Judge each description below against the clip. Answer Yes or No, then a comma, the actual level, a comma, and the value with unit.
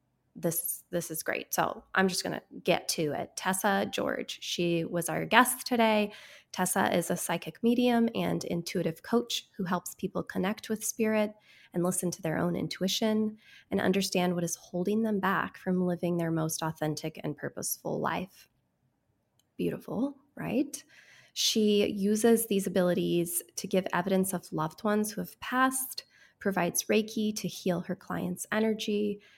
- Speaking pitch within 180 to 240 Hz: Yes, high, 190 Hz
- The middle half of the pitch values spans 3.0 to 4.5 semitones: Yes, average, 3.7 semitones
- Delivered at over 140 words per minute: Yes, average, 155 wpm